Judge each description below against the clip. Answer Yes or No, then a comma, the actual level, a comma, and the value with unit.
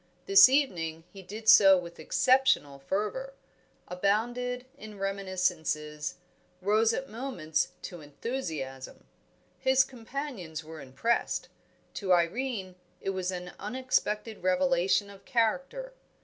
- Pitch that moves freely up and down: Yes, wide, 6.0 semitones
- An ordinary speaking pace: No, slow, 105 wpm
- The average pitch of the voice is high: Yes, high, 195 Hz